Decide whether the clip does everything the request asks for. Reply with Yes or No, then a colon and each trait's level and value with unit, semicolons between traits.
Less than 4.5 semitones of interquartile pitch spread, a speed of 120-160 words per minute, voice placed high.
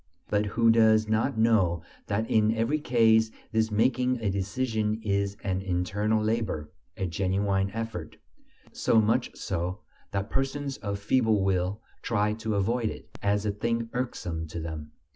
No: average, 2.7 semitones; average, 150 wpm; low, 105 Hz